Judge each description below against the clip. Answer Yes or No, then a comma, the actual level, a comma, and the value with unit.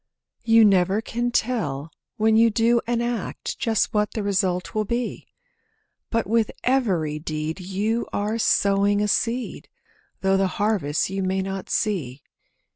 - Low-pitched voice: No, high, 205 Hz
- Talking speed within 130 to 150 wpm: Yes, average, 145 wpm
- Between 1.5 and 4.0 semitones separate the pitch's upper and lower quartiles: Yes, average, 3.3 semitones